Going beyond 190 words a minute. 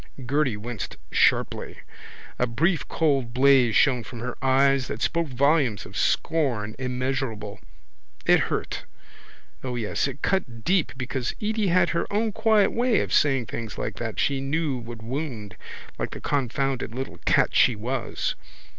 No: average, 145 wpm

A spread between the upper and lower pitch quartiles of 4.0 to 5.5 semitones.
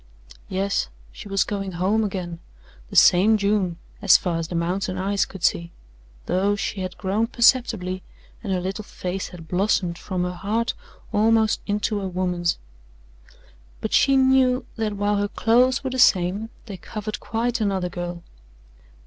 No: average, 3.3 semitones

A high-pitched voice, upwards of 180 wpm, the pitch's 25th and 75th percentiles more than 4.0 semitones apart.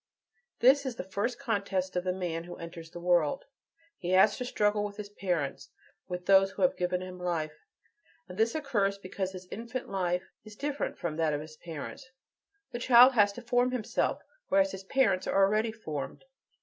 Yes: high, 195 Hz; average, 190 wpm; average, 4.5 semitones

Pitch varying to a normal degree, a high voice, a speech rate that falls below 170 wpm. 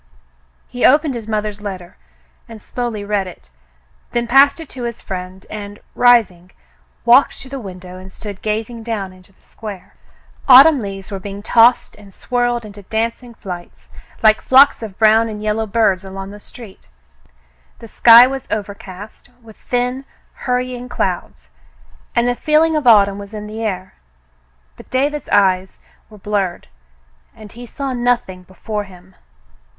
Yes: average, 3.8 semitones; high, 215 Hz; average, 155 wpm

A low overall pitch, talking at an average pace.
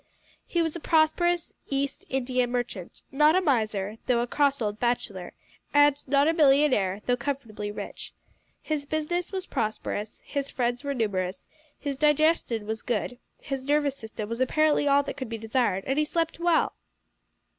No: very high, 270 Hz; average, 165 wpm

